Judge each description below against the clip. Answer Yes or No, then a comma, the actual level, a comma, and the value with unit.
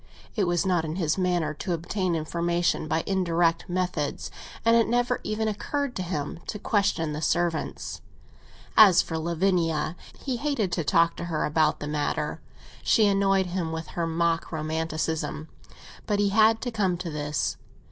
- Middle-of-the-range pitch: Yes, medium, 175 Hz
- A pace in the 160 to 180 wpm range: Yes, average, 165 wpm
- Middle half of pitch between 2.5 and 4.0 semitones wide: Yes, average, 3.5 semitones